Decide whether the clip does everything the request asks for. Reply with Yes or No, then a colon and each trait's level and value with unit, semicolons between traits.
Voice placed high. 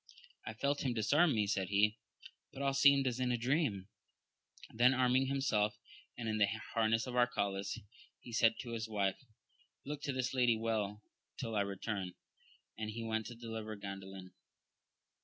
No: low, 115 Hz